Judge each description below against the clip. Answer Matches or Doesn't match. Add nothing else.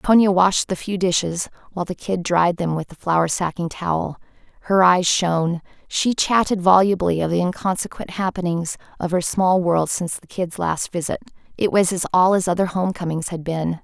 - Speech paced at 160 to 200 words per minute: Matches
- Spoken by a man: Doesn't match